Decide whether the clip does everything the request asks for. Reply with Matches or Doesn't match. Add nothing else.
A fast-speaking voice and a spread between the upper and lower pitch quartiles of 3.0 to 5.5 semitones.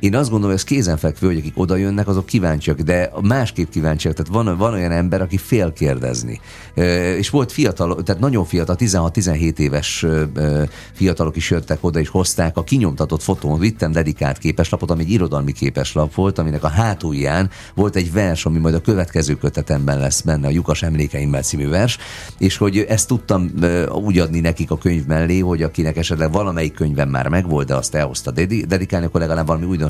Matches